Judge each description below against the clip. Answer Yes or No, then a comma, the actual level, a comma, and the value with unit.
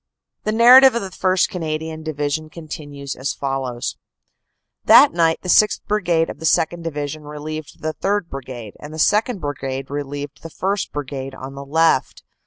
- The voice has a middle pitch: Yes, medium, 155 Hz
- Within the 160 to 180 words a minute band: Yes, average, 165 wpm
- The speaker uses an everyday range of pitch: Yes, average, 3.6 semitones